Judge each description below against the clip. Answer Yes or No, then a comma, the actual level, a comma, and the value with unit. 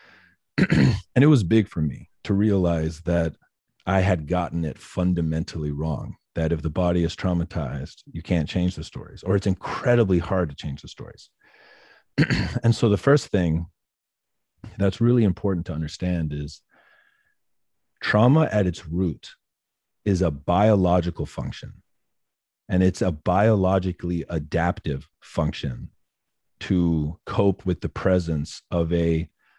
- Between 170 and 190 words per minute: No, slow, 135 wpm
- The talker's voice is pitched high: No, very low, 90 Hz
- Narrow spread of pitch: No, average, 3.4 semitones